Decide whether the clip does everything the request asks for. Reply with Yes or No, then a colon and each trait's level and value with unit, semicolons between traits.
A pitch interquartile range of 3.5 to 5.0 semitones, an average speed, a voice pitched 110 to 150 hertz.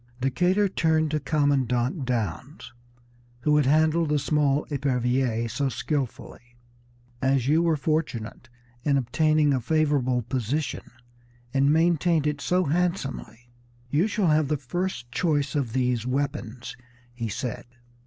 No: average, 3.8 semitones; slow, 125 wpm; medium, 140 Hz